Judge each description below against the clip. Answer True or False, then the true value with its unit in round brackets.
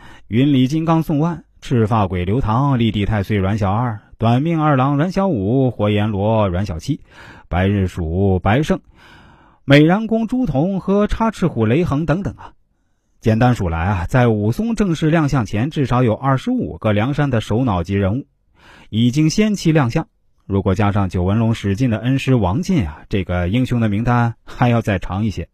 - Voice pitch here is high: False (120 Hz)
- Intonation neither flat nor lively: False (6.2 semitones)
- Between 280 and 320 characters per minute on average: False (265 characters per minute)